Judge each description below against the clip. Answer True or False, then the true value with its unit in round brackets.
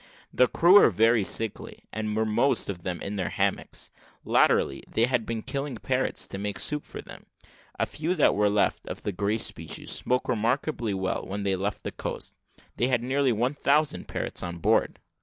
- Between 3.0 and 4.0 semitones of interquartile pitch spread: False (4.4 semitones)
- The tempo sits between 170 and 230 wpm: True (195 wpm)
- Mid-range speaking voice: False (110 Hz)